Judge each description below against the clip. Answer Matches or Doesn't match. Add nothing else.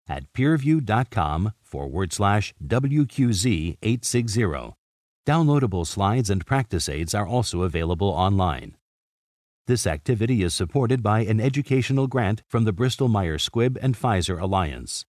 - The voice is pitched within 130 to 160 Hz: Doesn't match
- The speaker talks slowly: Matches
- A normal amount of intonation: Doesn't match